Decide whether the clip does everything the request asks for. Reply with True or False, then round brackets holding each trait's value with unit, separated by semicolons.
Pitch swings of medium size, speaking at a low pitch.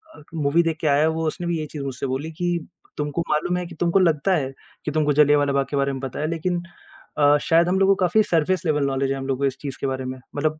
False (3.5 semitones; 150 Hz)